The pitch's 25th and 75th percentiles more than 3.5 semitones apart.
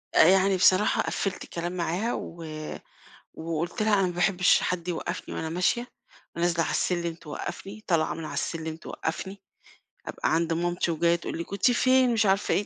No: average, 2.9 semitones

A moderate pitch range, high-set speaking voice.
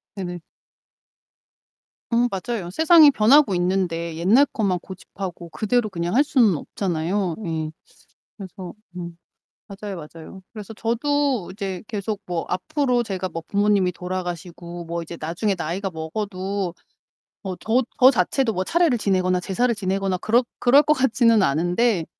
Yes: average, 4.6 semitones; high, 195 Hz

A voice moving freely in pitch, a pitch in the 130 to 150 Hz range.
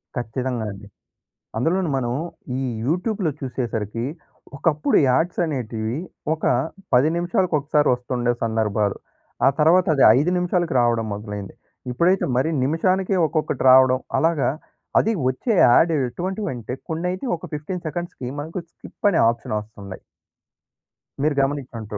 Yes: wide, 6.4 semitones; low, 135 Hz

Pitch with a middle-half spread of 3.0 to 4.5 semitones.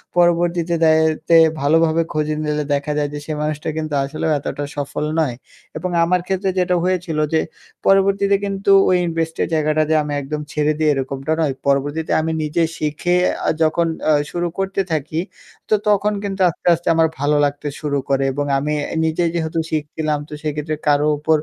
No: narrow, 2.4 semitones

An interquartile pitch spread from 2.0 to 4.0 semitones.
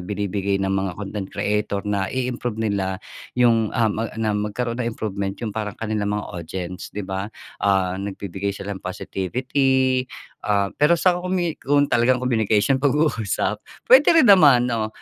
No: average, 4.4 semitones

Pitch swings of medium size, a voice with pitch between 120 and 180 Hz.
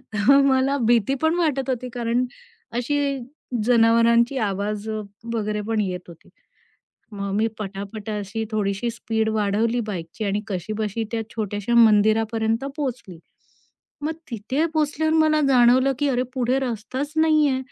No: average, 3.9 semitones; high, 230 Hz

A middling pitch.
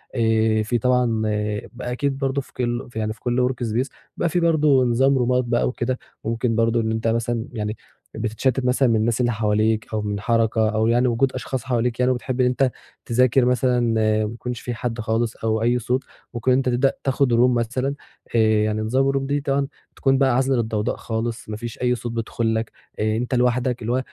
No: low, 120 Hz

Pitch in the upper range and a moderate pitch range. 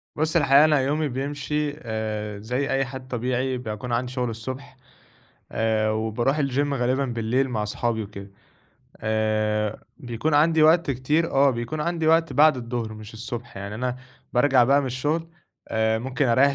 No: low, 125 Hz; average, 4.2 semitones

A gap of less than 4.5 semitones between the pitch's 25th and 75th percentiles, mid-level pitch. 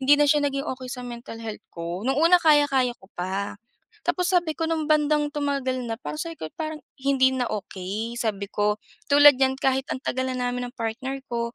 No: average, 3.9 semitones; very high, 260 Hz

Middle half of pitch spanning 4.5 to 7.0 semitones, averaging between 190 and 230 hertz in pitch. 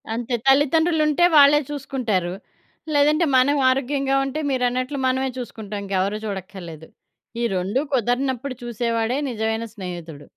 No: average, 5.1 semitones; very high, 250 Hz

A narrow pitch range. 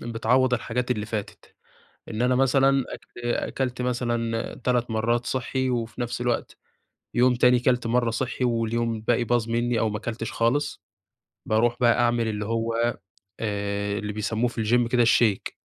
Yes: narrow, 1.6 semitones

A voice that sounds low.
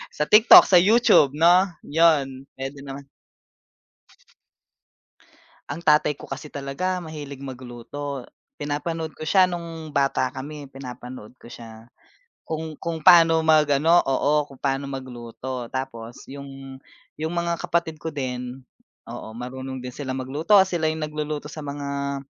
No: medium, 145 Hz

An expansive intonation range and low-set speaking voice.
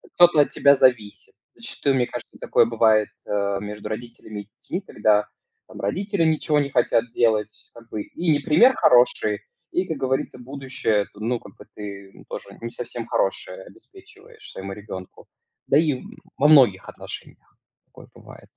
Yes: wide, 6.3 semitones; low, 125 Hz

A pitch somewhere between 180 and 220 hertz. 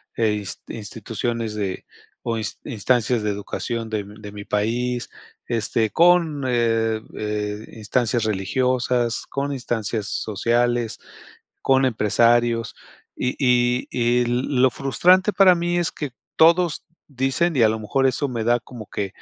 No: low, 120 Hz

